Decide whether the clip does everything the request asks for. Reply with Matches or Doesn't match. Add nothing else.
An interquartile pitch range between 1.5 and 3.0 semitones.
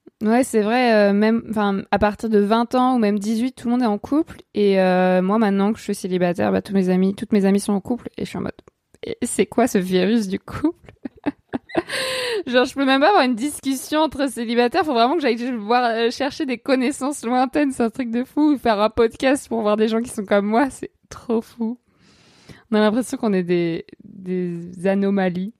Doesn't match